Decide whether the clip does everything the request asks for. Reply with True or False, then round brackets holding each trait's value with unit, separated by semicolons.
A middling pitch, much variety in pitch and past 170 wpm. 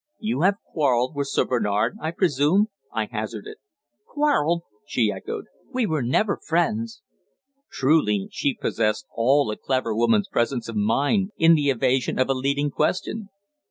False (145 Hz; 6.9 semitones; 150 wpm)